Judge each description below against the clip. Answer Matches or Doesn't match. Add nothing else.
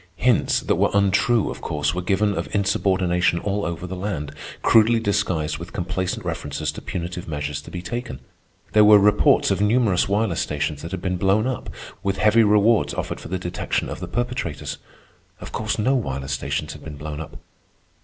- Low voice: Matches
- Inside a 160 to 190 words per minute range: Matches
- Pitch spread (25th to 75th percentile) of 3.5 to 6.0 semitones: Matches